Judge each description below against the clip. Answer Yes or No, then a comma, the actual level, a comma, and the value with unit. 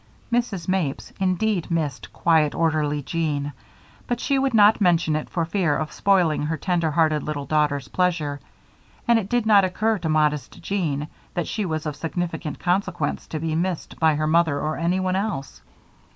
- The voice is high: No, medium, 165 Hz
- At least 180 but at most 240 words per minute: No, average, 170 wpm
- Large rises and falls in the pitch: No, average, 3.7 semitones